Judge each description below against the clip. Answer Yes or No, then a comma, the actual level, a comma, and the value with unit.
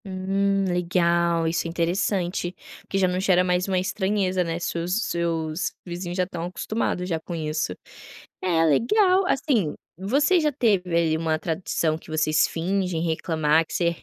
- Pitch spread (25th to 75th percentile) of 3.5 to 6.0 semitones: No, average, 2.7 semitones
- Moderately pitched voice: Yes, medium, 180 Hz